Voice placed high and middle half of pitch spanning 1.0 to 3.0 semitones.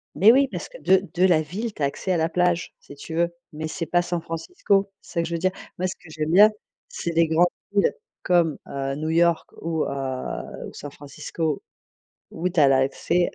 No: medium, 170 Hz; narrow, 2.6 semitones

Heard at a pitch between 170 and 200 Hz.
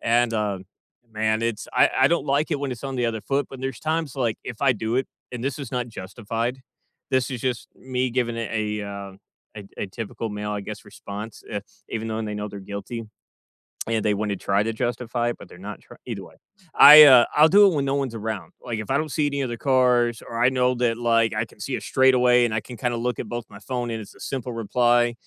No: low, 120 Hz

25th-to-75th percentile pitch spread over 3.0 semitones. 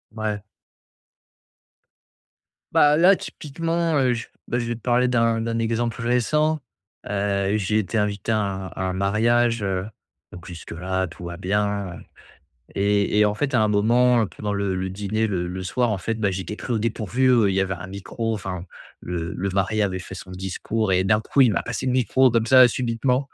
Yes: average, 3.7 semitones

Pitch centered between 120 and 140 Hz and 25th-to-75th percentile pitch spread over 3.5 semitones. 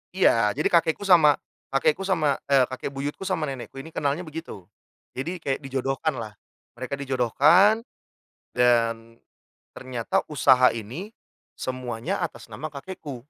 Yes: low, 135 Hz; average, 4.0 semitones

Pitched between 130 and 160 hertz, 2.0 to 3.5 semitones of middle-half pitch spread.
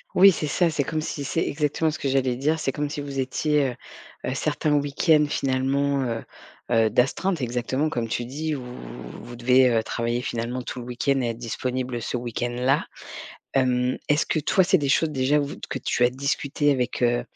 Yes: low, 135 Hz; average, 3.1 semitones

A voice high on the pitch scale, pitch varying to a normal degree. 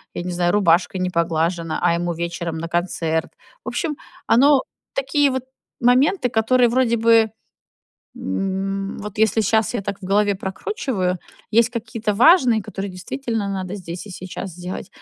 Yes: high, 200 Hz; average, 4.6 semitones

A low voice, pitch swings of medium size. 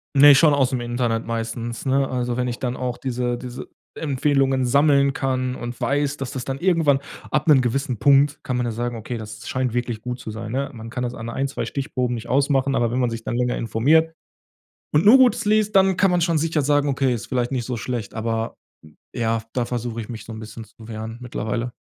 Yes: low, 125 Hz; average, 3.0 semitones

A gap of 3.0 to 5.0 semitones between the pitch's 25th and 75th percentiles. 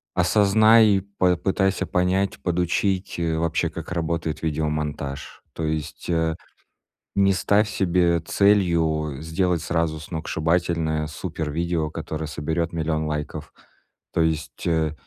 No: narrow, 2.5 semitones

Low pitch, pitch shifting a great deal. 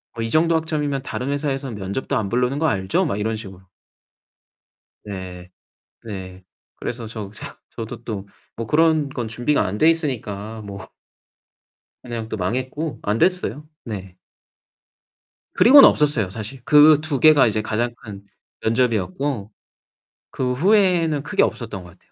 Yes: low, 120 Hz; wide, 6.1 semitones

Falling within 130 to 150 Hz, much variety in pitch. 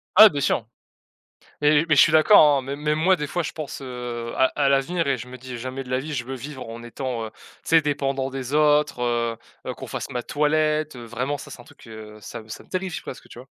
No: low, 135 Hz; average, 3.6 semitones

